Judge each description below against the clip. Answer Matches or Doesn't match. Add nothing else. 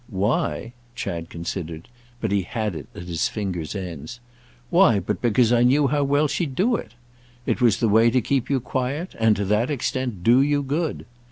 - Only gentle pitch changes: Doesn't match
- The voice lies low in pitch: Matches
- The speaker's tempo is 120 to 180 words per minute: Doesn't match